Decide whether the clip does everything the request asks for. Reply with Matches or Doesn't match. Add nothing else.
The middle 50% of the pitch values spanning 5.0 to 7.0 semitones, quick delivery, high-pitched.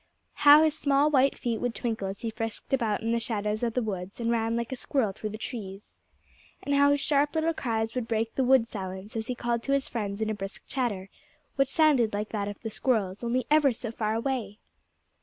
Doesn't match